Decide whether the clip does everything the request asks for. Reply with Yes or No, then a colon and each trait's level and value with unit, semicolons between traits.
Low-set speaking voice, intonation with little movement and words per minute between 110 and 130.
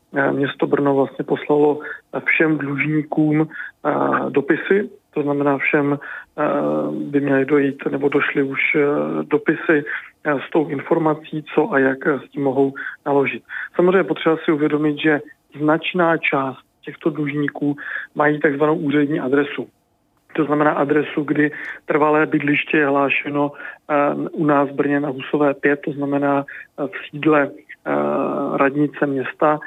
No: medium, 145 Hz; narrow, 1.5 semitones; average, 125 wpm